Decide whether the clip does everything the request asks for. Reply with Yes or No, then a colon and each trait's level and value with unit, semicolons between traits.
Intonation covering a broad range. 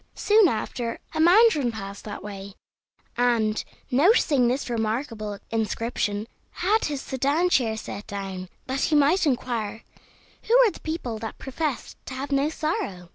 Yes: wide, 5.8 semitones